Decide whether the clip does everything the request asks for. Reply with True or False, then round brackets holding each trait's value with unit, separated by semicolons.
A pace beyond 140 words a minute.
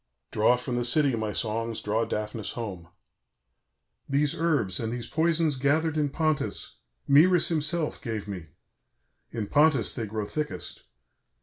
False (135 wpm)